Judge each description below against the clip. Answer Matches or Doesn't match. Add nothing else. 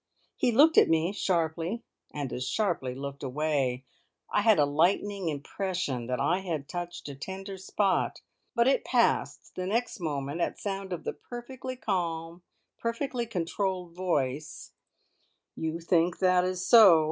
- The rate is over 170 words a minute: Doesn't match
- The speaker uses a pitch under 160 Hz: Doesn't match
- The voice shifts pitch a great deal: Doesn't match